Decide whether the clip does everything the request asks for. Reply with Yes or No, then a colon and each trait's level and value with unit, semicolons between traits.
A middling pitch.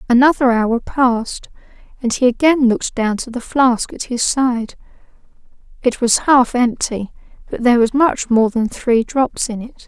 No: high, 245 Hz